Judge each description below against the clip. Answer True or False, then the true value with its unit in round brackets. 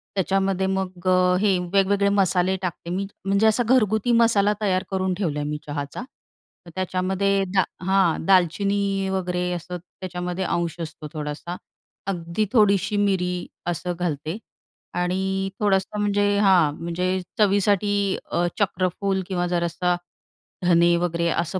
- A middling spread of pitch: False (2.1 semitones)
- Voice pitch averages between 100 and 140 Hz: False (185 Hz)